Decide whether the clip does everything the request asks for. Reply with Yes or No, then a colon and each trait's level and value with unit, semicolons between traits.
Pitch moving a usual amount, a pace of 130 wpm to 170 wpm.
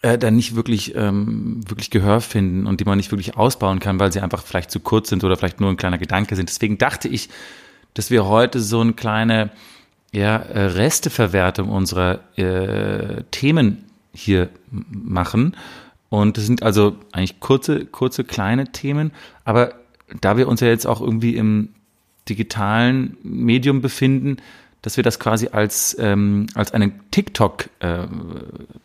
Yes: average, 3.0 semitones; average, 155 wpm